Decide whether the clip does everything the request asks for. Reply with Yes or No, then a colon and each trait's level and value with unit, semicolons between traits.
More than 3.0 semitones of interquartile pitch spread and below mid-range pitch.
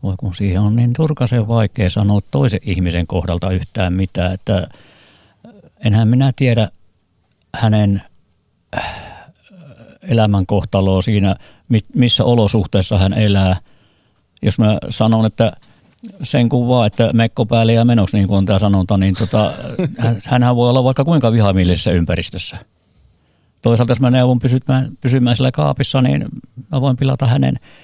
Yes: average, 4.3 semitones; low, 110 Hz